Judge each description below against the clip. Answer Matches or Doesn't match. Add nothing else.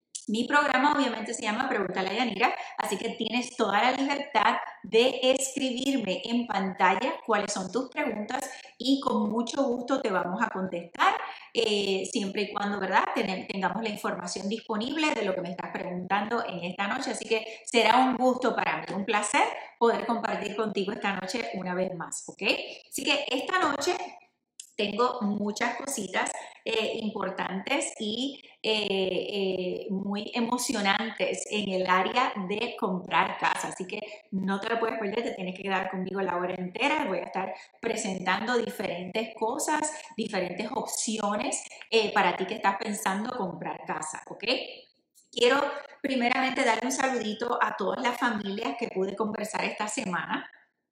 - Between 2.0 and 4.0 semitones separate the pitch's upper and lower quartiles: Doesn't match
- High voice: Matches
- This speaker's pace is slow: Doesn't match